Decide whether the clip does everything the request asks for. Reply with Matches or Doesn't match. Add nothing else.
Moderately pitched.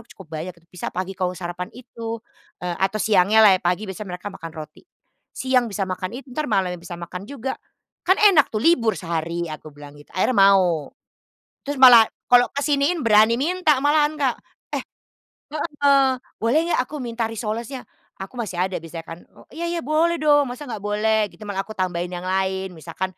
Doesn't match